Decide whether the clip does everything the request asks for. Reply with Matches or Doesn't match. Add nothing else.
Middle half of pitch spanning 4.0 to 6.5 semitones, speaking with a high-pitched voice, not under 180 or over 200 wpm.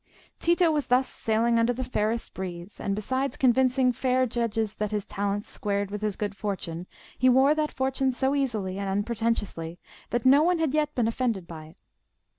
Matches